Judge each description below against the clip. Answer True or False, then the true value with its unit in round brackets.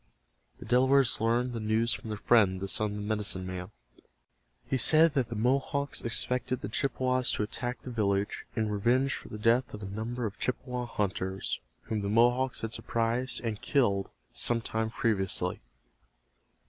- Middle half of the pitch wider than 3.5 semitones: False (3.2 semitones)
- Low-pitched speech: True (115 Hz)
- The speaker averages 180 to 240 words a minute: False (170 wpm)